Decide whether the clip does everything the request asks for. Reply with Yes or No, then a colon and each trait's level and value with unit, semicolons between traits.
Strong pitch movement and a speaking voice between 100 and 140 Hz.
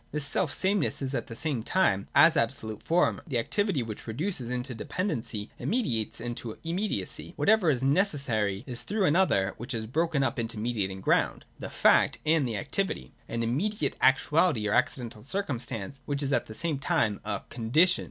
Yes: wide, 6.5 semitones; low, 135 Hz